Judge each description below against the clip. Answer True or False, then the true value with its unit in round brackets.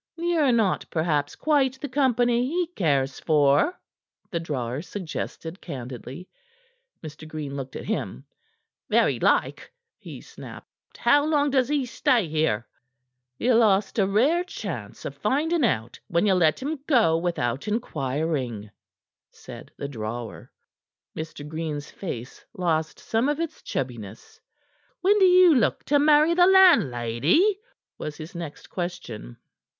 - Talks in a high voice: False (175 Hz)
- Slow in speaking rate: True (130 wpm)